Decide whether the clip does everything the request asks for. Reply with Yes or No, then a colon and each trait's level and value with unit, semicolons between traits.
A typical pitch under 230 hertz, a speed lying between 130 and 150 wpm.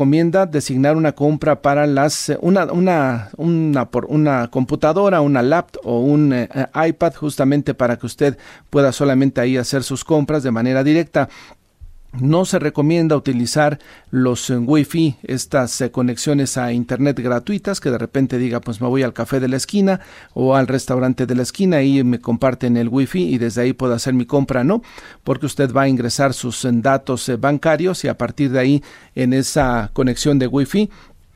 No: low, 135 Hz; average, 180 wpm